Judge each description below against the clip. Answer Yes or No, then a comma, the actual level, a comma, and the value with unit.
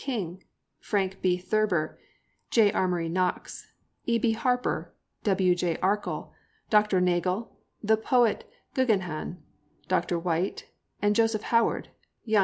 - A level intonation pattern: No, average, 3.5 semitones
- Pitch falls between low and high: No, high, 195 Hz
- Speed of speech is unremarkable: No, slow, 105 wpm